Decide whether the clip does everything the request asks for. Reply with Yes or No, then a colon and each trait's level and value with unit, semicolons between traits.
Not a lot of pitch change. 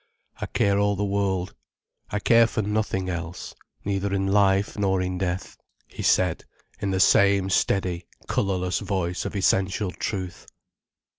Yes: narrow, 1.5 semitones